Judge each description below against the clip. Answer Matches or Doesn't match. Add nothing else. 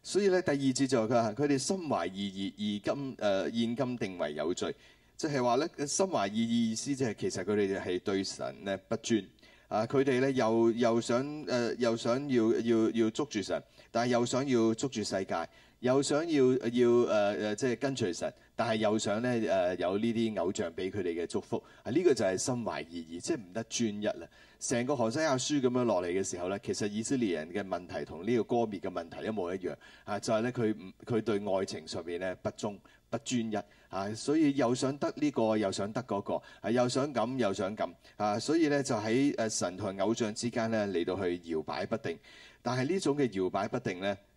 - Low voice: Matches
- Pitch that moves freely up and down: Doesn't match